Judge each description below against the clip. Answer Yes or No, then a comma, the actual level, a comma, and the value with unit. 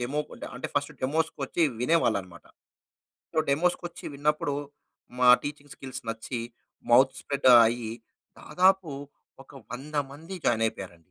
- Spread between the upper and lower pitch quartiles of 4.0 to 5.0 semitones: Yes, average, 4.4 semitones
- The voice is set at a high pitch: No, medium, 140 Hz